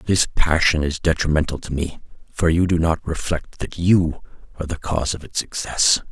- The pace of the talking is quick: No, average, 185 wpm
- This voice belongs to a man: Yes, male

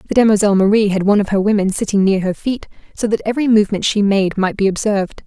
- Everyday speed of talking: No, fast, 240 wpm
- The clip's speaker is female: Yes, female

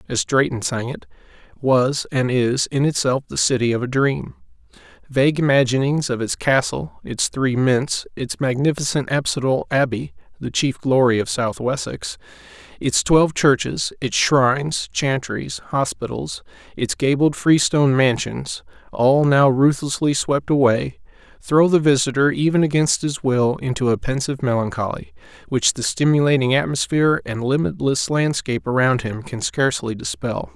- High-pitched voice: No, low, 135 Hz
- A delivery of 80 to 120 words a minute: No, slow, 135 wpm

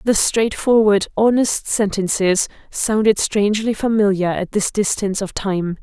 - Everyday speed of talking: No, slow, 125 wpm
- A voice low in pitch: No, high, 205 Hz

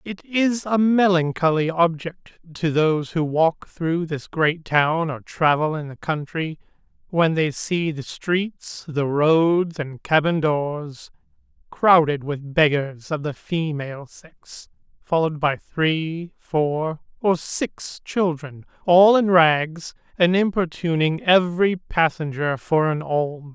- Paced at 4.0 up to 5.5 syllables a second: No, 3.5 syllables/s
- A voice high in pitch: No, medium, 160 Hz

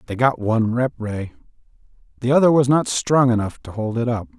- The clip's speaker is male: Yes, male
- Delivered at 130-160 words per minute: No, fast, 205 wpm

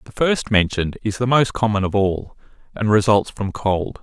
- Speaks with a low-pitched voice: Yes, low, 105 Hz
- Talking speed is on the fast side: No, average, 195 wpm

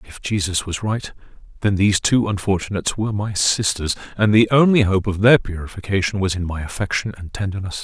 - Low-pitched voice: Yes, low, 100 Hz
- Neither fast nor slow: Yes, average, 185 wpm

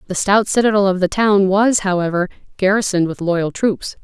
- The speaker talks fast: No, average, 180 wpm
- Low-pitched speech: No, high, 195 Hz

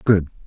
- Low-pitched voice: Yes, very low, 90 Hz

